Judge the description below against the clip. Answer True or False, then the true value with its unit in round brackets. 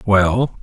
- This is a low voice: True (105 Hz)